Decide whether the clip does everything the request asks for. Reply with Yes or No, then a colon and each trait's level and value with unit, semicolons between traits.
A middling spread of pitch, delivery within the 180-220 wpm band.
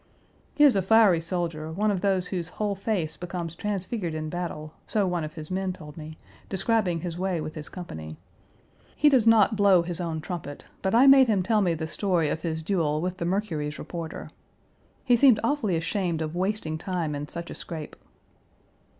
Yes: average, 4.1 semitones; average, 195 wpm